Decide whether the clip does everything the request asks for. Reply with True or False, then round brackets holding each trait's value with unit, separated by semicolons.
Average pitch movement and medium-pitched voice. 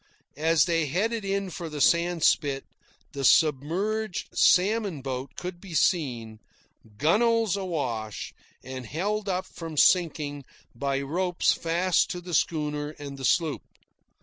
True (4.7 semitones; 165 Hz)